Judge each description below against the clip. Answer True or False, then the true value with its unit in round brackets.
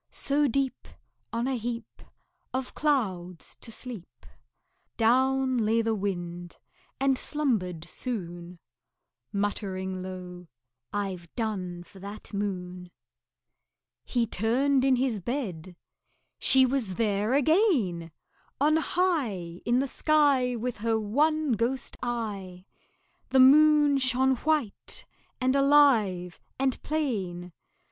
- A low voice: False (230 Hz)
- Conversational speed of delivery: False (105 wpm)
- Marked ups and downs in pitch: True (6.1 semitones)